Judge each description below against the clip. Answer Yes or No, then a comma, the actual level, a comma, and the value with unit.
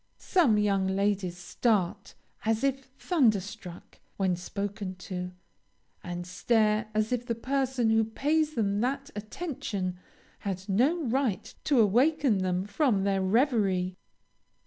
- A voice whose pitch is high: Yes, high, 215 Hz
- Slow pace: Yes, slow, 125 wpm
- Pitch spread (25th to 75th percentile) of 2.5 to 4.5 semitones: No, average, 5.0 semitones